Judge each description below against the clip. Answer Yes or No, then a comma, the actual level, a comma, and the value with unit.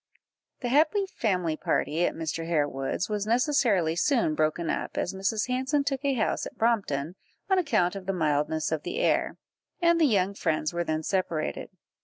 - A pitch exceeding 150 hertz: Yes, high, 190 Hz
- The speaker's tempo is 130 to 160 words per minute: No, average, 175 wpm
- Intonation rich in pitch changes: Yes, wide, 8.1 semitones